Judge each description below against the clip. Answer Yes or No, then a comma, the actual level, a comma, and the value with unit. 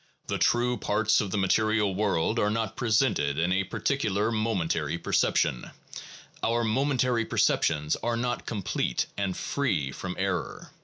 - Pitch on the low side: Yes, low, 105 Hz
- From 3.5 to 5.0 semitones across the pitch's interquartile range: Yes, average, 4.0 semitones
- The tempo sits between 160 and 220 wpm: No, average, 140 wpm